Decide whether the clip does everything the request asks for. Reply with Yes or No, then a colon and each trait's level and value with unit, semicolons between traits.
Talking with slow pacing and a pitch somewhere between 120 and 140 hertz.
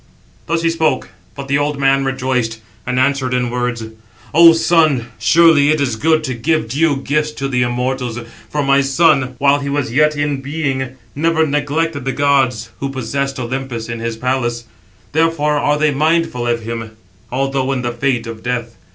No: average, 175 wpm; low, 135 Hz